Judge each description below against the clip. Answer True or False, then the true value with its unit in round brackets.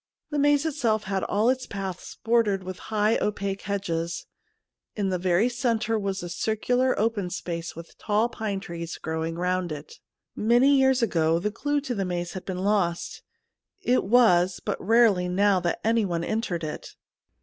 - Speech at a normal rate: True (165 wpm)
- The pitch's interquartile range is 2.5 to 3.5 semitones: False (4.5 semitones)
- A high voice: True (200 Hz)